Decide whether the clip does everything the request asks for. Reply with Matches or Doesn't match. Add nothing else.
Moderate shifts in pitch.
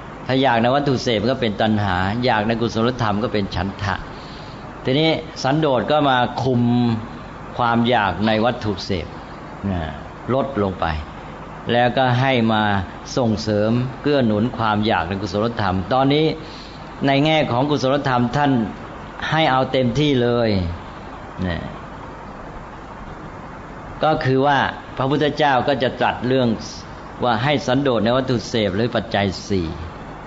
Matches